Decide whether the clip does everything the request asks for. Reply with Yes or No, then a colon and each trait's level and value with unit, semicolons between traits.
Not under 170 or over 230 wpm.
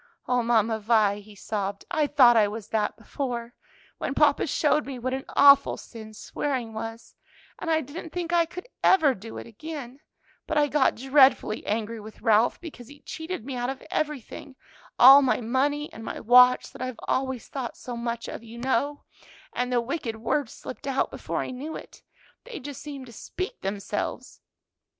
Yes: average, 180 wpm